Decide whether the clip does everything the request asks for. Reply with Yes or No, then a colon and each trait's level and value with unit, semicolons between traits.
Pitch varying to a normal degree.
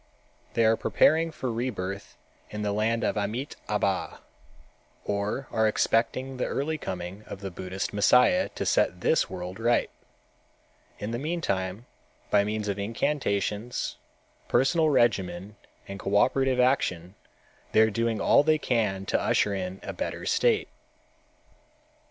Yes: average, 4.4 semitones